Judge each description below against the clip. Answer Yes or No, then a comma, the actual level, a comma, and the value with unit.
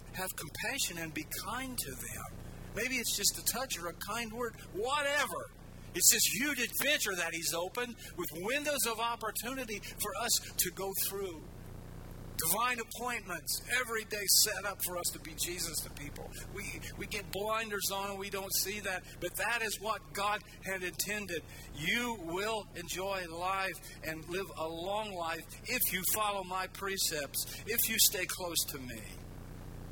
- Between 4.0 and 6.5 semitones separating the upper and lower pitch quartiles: Yes, average, 4.9 semitones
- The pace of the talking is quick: No, average, 165 wpm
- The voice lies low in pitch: No, high, 190 Hz